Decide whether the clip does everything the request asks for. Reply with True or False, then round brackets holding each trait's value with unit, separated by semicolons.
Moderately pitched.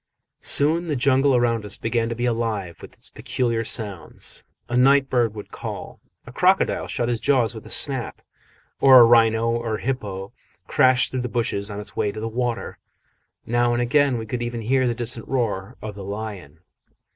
False (120 Hz)